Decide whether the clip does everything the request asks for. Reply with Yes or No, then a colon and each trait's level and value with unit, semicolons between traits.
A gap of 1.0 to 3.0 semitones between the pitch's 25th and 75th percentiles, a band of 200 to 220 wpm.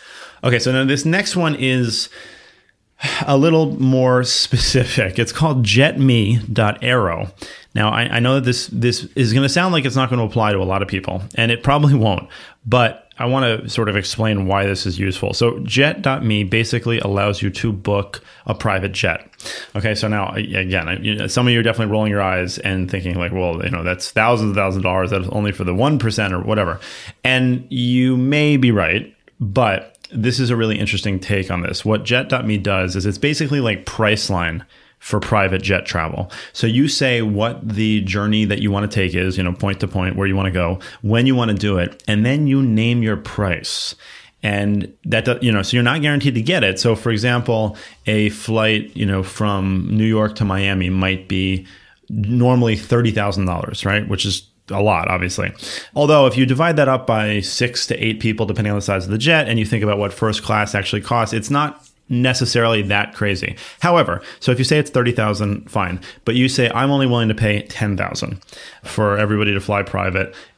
No: average, 3.8 semitones; fast, 205 wpm